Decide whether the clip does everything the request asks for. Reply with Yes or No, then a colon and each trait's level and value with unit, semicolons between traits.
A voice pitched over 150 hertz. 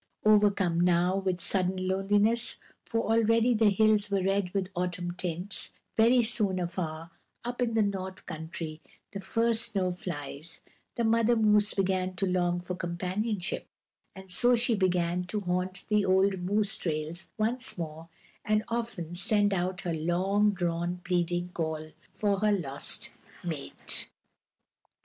Yes: high, 190 Hz